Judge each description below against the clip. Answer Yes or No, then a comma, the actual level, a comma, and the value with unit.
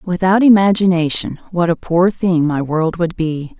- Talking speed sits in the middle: Yes, average, 165 wpm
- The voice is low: No, medium, 175 Hz